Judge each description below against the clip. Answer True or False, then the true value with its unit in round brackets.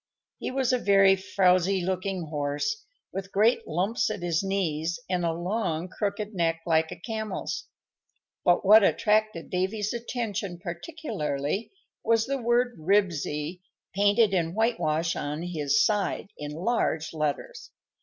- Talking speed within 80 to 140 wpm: True (135 wpm)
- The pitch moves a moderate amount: True (4.7 semitones)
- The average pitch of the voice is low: False (190 Hz)